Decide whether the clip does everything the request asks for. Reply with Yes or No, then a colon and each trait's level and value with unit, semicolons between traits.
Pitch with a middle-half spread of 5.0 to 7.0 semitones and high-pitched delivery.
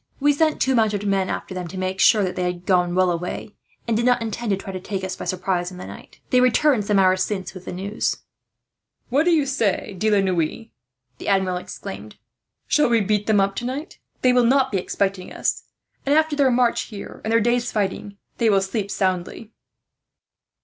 No: average, 4.4 semitones; high, 205 Hz